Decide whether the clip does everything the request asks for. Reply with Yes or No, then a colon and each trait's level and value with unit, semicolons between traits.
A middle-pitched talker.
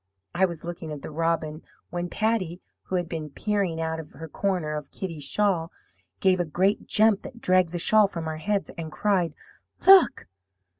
Yes: medium, 175 Hz